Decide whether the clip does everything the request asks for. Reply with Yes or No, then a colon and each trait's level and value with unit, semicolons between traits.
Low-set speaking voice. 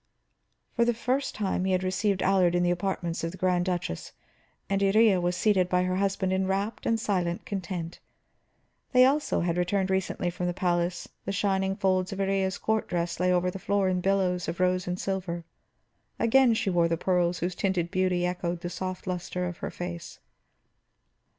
No: medium, 185 Hz